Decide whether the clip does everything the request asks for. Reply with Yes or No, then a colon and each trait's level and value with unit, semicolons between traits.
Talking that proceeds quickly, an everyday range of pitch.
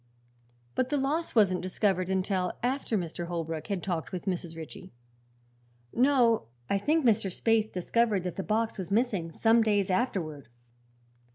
No: average, 150 wpm; average, 4.4 semitones